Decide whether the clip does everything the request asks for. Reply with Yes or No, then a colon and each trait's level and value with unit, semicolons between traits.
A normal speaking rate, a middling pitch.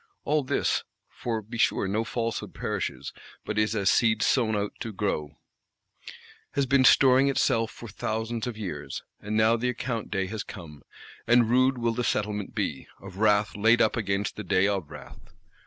No: average, 175 wpm; low, 110 Hz